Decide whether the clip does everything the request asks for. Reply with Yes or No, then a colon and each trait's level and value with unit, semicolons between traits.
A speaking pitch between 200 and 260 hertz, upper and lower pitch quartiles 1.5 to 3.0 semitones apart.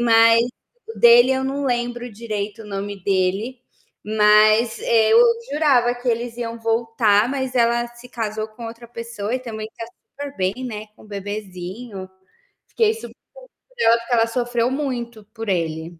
Yes: high, 230 Hz; narrow, 2.4 semitones